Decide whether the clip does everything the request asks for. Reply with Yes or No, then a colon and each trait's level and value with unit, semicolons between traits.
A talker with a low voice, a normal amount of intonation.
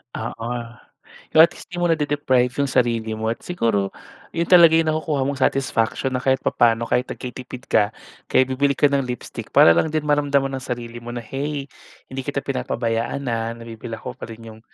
Yes: low, 130 Hz; average, 3.6 semitones